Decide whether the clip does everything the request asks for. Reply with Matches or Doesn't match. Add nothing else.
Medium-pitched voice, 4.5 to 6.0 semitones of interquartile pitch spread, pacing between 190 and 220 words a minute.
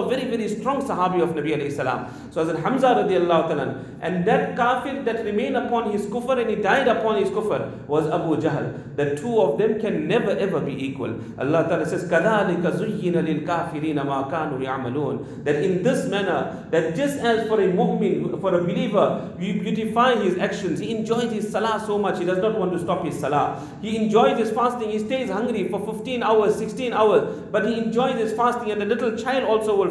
Doesn't match